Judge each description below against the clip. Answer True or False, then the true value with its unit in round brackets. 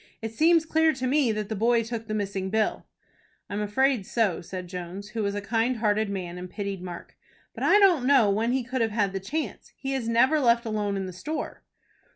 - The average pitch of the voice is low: False (220 Hz)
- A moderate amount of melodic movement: True (4.3 semitones)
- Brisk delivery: True (225 wpm)